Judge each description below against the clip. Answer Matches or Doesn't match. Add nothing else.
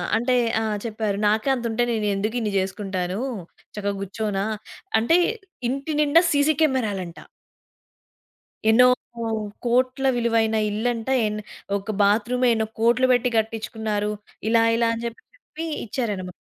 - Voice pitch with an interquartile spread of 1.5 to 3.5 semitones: Matches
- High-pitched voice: Matches